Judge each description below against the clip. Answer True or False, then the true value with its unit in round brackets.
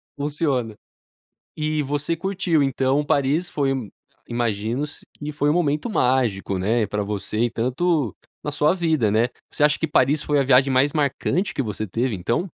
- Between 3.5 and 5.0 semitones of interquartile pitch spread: True (4.2 semitones)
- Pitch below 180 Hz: True (140 Hz)